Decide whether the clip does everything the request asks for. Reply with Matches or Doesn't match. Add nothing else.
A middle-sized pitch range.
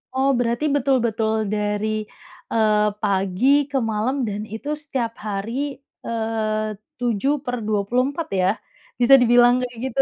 Matches